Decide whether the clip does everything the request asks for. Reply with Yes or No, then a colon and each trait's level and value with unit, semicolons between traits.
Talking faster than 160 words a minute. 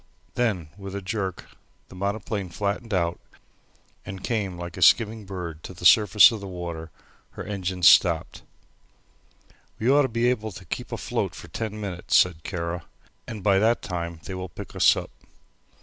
Yes: average, 170 wpm